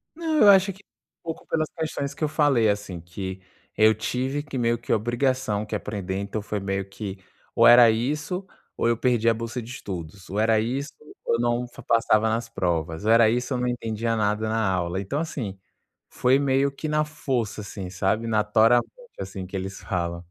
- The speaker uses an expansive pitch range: No, average, 4.6 semitones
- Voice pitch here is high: No, low, 115 Hz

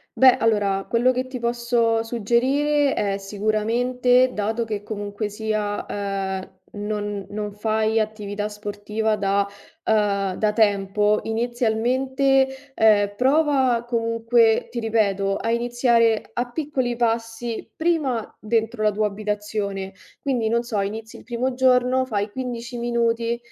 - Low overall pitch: No, high, 225 Hz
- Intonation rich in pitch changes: No, average, 2.7 semitones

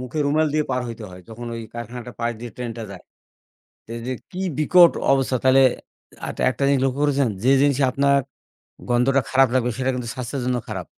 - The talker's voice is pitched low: Yes, low, 130 Hz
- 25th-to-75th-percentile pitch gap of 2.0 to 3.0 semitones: Yes, narrow, 2.6 semitones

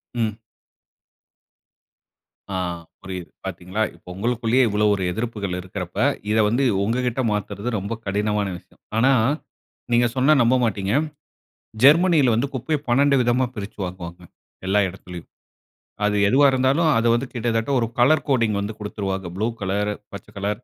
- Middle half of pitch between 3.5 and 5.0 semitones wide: Yes, average, 4.0 semitones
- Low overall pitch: Yes, low, 110 Hz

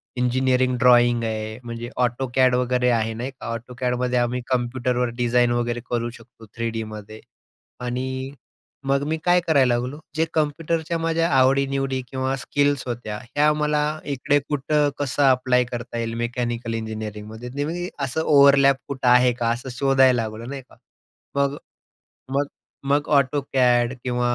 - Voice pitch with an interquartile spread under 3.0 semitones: Yes, narrow, 2.4 semitones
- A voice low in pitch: Yes, low, 125 Hz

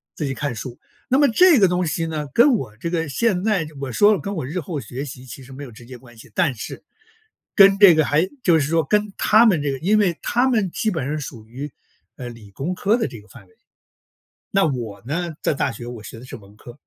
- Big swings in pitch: Yes, wide, 7.7 semitones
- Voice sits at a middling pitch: Yes, medium, 150 Hz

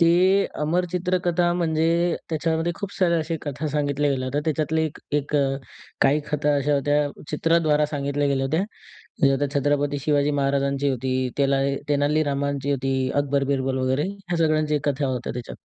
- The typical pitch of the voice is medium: Yes, medium, 145 Hz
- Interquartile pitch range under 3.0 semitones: Yes, narrow, 2.4 semitones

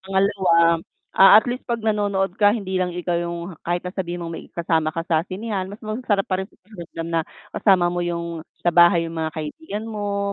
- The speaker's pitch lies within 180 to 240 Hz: Yes, medium, 185 Hz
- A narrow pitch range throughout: No, average, 3.1 semitones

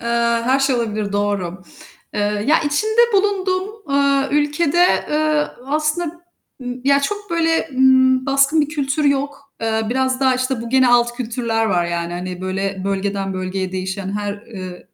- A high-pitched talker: Yes, very high, 260 Hz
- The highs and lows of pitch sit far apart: Yes, wide, 6.7 semitones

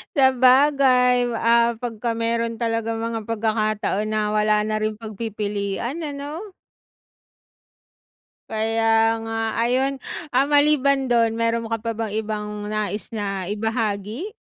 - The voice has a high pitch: Yes, high, 225 Hz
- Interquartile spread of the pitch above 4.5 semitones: No, average, 2.7 semitones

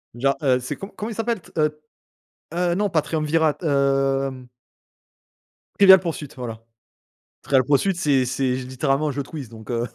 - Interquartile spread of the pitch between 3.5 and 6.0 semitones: Yes, average, 4.0 semitones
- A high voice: No, medium, 140 Hz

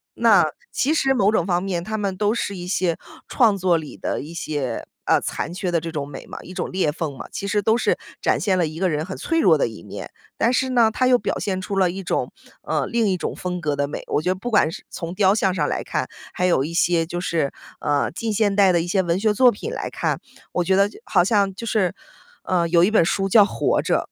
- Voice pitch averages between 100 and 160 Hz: No, medium, 185 Hz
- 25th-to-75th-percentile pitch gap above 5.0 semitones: No, average, 3.6 semitones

